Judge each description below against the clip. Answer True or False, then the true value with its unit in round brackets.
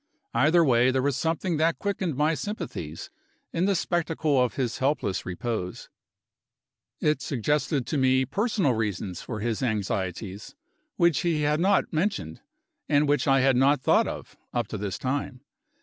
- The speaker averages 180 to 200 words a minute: False (155 wpm)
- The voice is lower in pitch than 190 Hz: True (135 Hz)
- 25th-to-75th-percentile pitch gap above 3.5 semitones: True (5.5 semitones)